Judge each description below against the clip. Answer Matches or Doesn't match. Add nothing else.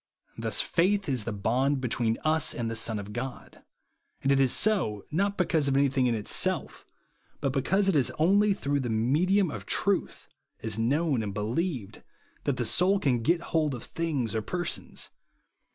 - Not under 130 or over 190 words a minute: Matches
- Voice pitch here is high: Doesn't match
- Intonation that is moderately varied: Doesn't match